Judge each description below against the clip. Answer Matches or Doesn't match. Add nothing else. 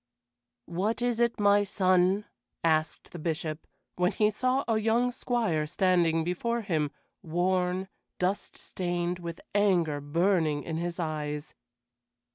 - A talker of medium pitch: Matches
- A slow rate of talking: Matches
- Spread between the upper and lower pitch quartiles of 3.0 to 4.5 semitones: Matches